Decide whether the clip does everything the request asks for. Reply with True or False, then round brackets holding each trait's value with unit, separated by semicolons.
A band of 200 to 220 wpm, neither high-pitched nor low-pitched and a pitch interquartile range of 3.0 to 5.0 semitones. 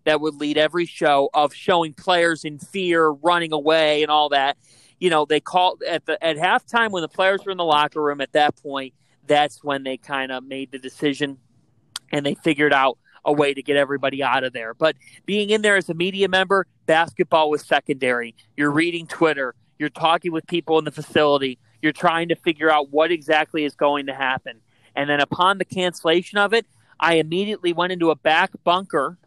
True (205 wpm; 155 Hz; 3.4 semitones)